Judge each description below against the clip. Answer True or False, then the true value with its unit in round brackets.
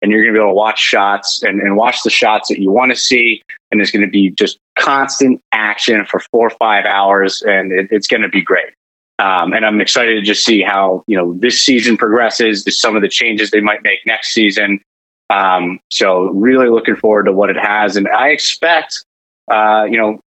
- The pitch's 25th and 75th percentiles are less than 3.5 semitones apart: True (2.4 semitones)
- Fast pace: True (215 wpm)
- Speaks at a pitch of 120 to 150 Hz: False (105 Hz)